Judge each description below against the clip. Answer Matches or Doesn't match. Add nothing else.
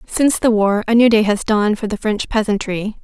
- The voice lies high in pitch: Matches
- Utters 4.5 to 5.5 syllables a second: Doesn't match